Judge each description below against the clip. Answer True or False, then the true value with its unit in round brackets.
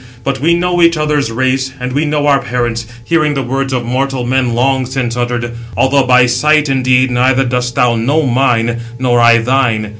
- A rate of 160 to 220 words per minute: True (190 wpm)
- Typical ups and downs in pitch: False (2.1 semitones)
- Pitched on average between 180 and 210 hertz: False (130 Hz)